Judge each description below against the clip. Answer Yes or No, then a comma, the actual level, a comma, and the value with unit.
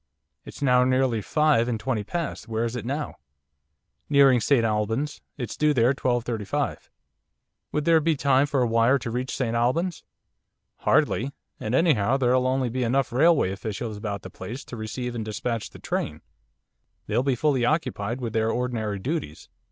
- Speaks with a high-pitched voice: No, low, 125 Hz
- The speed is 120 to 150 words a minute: No, average, 165 wpm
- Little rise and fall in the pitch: No, average, 3.5 semitones